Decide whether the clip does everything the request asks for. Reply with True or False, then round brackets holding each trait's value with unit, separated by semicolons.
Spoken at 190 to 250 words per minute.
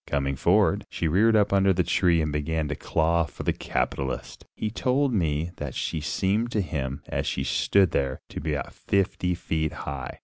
True (195 wpm)